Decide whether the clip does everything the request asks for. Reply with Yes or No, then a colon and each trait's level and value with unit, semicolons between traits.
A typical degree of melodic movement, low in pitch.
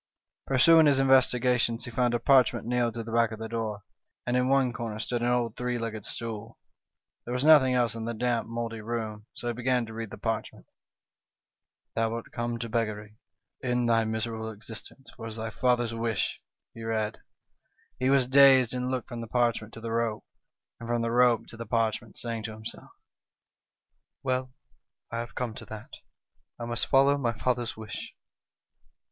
No: narrow, 1.7 semitones; low, 115 Hz